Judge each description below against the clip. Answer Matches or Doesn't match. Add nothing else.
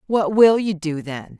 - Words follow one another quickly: Matches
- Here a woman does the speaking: Matches